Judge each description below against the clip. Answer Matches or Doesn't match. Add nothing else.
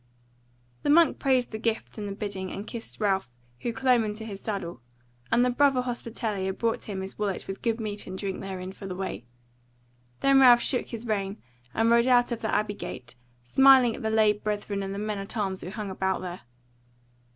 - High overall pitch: Matches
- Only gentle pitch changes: Doesn't match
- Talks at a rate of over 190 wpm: Matches